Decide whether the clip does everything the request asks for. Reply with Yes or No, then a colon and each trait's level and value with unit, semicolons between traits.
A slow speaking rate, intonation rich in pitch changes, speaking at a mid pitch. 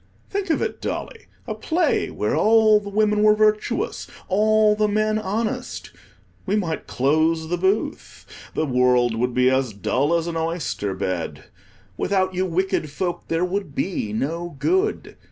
No: average, 155 wpm; wide, 6.8 semitones; medium, 180 Hz